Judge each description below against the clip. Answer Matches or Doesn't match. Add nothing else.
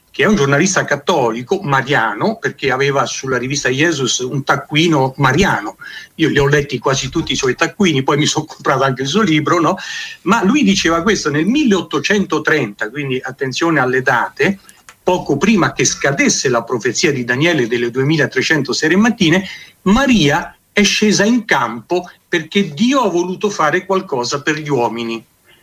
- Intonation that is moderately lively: Doesn't match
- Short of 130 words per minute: Doesn't match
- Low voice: Doesn't match